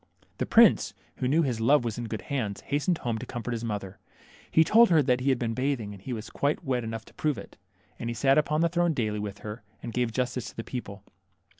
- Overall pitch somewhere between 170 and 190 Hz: No, low, 120 Hz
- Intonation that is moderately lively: Yes, average, 4.1 semitones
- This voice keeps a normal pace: No, fast, 245 wpm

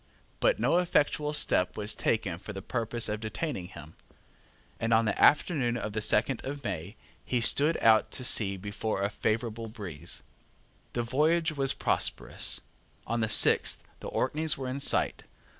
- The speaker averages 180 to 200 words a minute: No, average, 160 wpm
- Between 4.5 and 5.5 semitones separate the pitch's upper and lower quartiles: Yes, average, 5.0 semitones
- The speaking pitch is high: No, low, 115 Hz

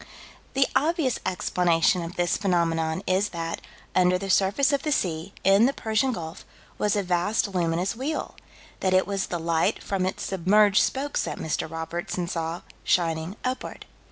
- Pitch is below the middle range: No, medium, 185 Hz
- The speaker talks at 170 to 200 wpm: No, average, 160 wpm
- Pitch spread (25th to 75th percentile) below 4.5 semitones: Yes, average, 3.7 semitones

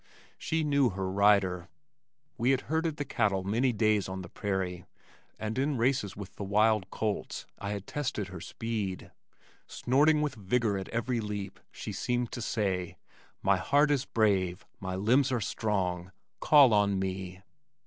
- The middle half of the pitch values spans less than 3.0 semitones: No, average, 4.6 semitones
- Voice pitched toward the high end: No, low, 105 Hz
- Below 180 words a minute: Yes, average, 160 wpm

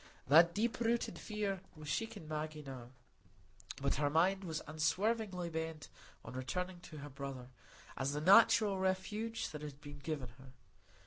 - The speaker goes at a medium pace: Yes, average, 150 wpm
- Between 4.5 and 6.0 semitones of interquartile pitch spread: Yes, average, 5.1 semitones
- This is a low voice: No, medium, 160 Hz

